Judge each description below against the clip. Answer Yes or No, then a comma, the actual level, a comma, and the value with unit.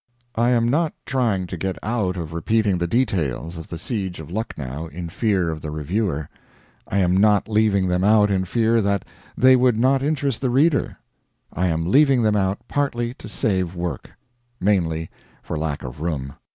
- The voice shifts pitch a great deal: Yes, wide, 5.7 semitones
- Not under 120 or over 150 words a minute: No, average, 180 wpm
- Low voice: Yes, low, 100 Hz